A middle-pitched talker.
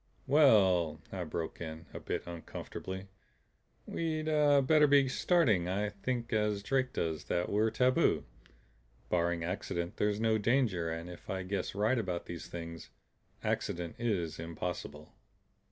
No: low, 100 Hz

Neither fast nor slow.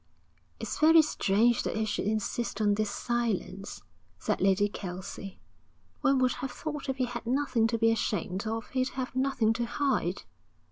Yes: average, 170 wpm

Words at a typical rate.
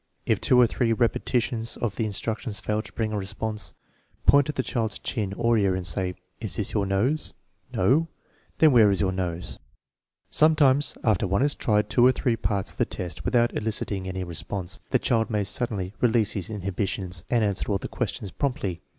No: fast, 210 wpm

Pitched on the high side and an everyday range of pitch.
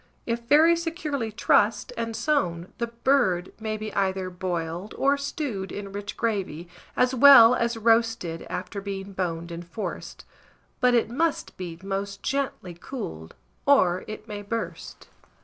Yes: high, 215 Hz; average, 4.8 semitones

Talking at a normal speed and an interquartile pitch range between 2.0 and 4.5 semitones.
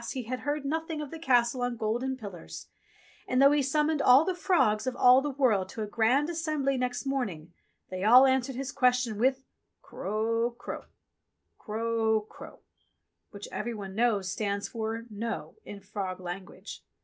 Yes: average, 175 wpm; average, 4.1 semitones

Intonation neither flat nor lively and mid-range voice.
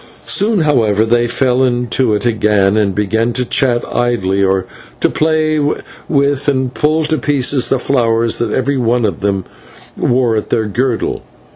No: average, 3.8 semitones; low, 120 Hz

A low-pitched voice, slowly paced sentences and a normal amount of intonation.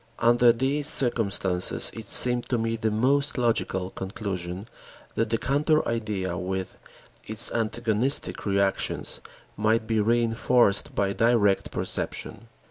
Yes: low, 115 Hz; slow, 120 wpm; average, 3.3 semitones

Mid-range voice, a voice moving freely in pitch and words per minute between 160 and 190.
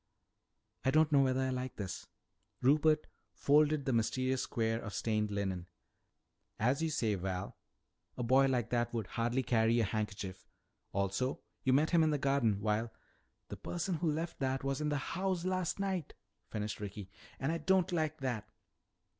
No: low, 130 Hz; wide, 5.7 semitones; average, 170 wpm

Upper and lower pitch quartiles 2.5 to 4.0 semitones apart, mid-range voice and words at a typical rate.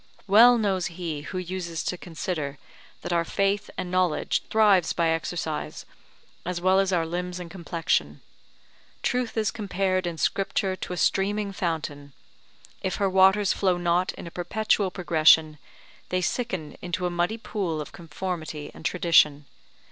Yes: average, 2.8 semitones; medium, 180 Hz; average, 150 wpm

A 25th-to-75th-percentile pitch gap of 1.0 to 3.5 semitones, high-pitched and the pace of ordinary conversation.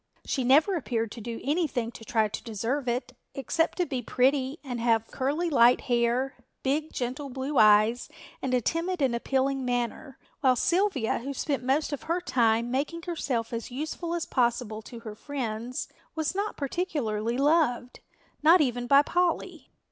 No: average, 4.2 semitones; very high, 260 Hz; average, 165 wpm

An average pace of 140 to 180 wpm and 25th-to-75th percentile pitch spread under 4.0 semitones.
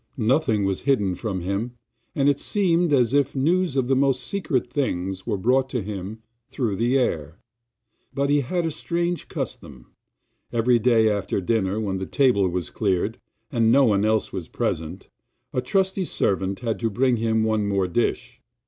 No: average, 175 wpm; wide, 5.5 semitones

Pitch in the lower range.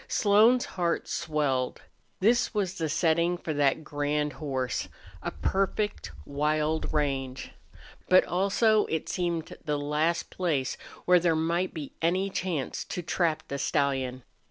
No: medium, 160 Hz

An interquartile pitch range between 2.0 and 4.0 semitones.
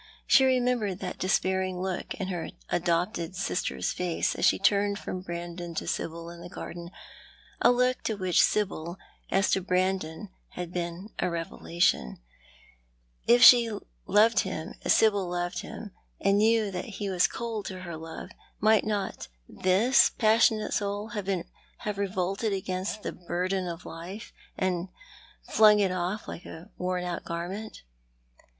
Yes: average, 3.1 semitones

